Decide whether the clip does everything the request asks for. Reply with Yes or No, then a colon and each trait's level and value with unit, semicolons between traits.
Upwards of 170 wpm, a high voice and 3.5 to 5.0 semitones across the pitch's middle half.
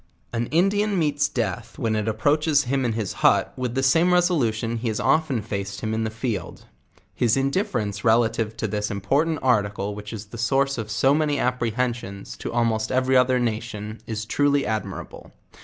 No: average, 180 wpm; low, 115 Hz; average, 4.0 semitones